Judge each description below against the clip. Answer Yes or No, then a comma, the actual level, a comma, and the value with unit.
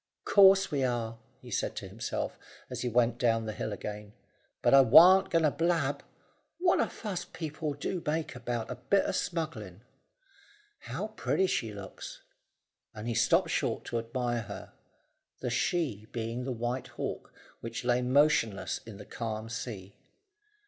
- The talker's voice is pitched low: Yes, low, 125 Hz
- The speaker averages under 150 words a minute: No, average, 160 wpm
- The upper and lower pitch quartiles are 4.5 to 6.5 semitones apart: Yes, average, 5.3 semitones